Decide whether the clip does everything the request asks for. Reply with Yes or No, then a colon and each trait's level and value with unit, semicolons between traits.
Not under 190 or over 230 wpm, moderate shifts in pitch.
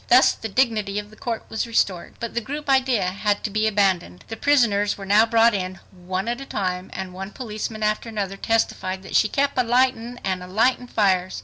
Yes: fast, 205 wpm; average, 3.6 semitones